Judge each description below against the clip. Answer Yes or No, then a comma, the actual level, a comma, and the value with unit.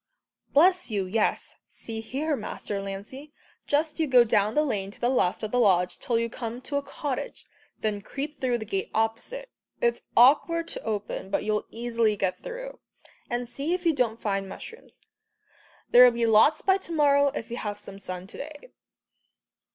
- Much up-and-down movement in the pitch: Yes, wide, 5.8 semitones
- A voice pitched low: No, high, 240 Hz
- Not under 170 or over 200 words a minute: Yes, average, 180 wpm